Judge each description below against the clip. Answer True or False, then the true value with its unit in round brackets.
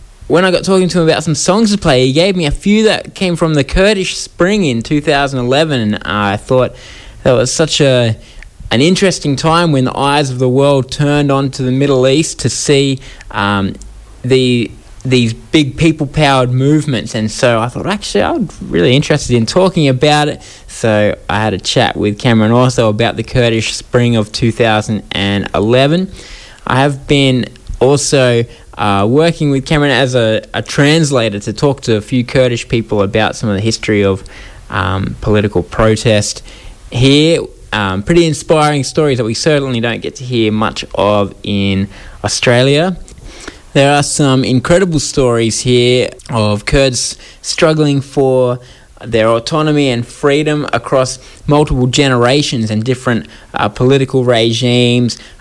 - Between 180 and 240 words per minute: False (160 wpm)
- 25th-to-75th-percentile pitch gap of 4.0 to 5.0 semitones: True (4.7 semitones)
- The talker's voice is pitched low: True (125 Hz)